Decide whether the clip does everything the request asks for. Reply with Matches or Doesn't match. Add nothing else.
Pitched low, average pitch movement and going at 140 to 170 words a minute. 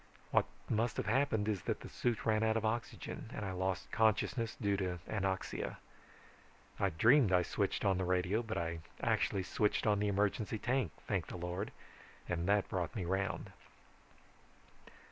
Matches